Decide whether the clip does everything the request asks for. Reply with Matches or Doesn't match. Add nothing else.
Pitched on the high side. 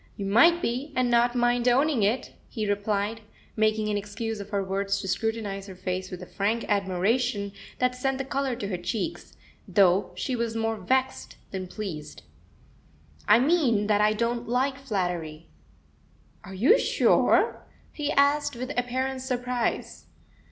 Matches